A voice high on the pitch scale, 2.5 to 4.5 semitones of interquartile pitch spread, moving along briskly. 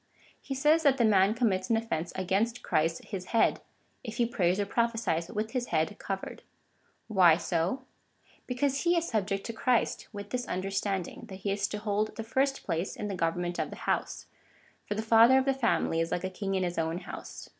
Yes: high, 205 Hz; average, 4.1 semitones; fast, 210 wpm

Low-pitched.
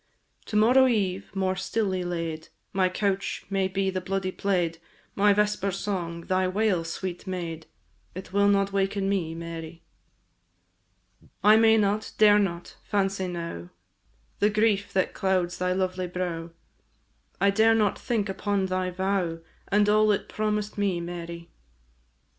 No: high, 190 Hz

